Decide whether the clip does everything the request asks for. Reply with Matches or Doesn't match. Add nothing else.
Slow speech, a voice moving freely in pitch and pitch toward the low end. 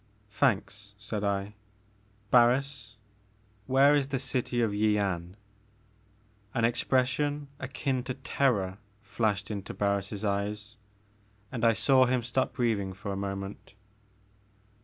Doesn't match